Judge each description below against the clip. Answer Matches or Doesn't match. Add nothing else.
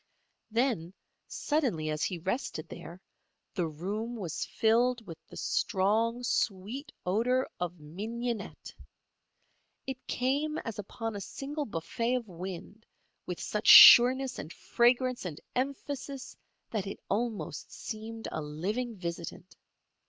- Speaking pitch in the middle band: Doesn't match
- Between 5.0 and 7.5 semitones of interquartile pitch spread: Matches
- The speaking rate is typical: Doesn't match